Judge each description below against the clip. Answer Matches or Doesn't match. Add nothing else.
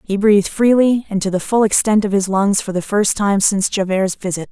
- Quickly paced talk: Matches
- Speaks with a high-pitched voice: Matches